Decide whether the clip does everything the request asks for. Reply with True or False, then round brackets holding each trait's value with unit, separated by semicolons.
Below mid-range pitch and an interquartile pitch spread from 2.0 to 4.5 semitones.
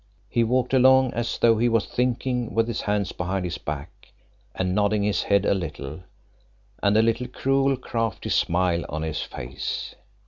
False (105 Hz; 5.0 semitones)